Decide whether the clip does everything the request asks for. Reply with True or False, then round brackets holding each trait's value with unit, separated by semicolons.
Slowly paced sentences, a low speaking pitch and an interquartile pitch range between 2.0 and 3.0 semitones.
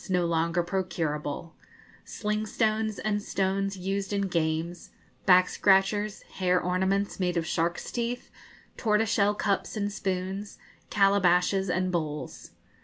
False (120 wpm; 190 Hz; 2.6 semitones)